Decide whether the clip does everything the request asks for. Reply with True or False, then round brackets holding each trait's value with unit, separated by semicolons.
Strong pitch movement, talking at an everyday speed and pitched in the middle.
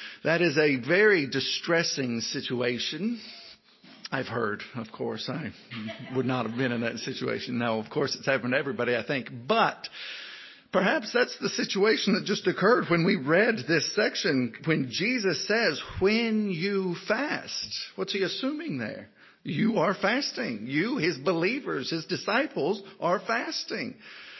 True (8.4 semitones; 150 wpm; 175 Hz)